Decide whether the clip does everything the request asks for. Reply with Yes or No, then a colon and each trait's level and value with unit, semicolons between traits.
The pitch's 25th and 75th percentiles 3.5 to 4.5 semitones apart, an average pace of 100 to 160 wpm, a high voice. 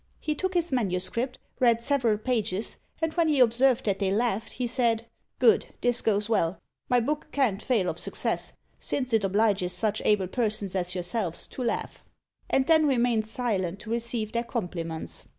No: average, 4.1 semitones; average, 175 wpm; high, 230 Hz